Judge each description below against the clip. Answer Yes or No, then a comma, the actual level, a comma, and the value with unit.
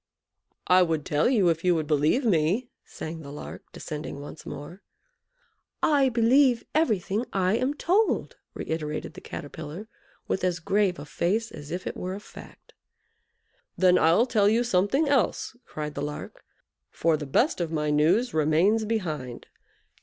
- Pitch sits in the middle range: Yes, medium, 180 Hz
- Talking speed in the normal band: Yes, average, 155 wpm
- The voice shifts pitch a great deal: Yes, wide, 6.7 semitones